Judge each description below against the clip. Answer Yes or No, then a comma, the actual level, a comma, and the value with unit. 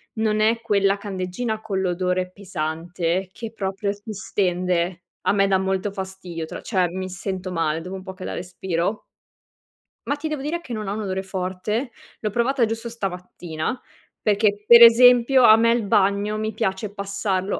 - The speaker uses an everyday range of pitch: Yes, average, 3.0 semitones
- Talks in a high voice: Yes, high, 195 Hz